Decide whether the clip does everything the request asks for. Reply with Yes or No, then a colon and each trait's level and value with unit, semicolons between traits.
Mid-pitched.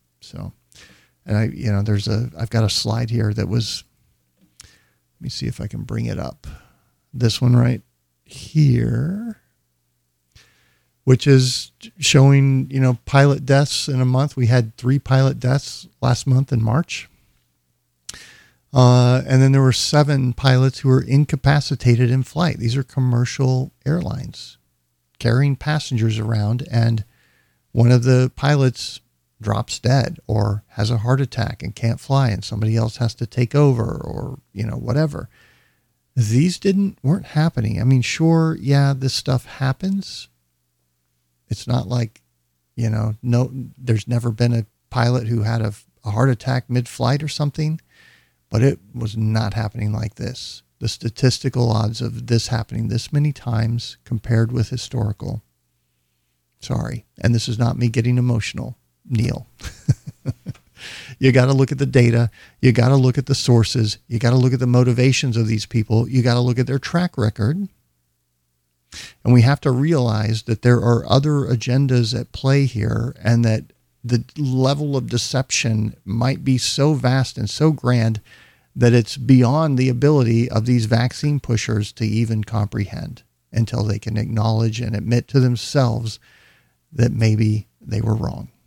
No: low, 120 Hz